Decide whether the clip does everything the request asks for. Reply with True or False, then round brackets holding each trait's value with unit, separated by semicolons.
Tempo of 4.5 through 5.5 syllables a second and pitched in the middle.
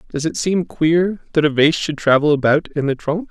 True (5.0 syllables/s; 155 Hz)